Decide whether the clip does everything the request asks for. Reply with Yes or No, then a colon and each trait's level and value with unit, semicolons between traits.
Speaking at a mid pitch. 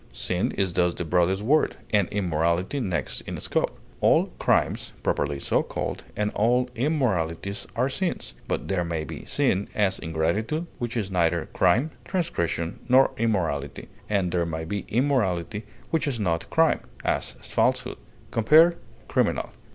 No: low, 100 Hz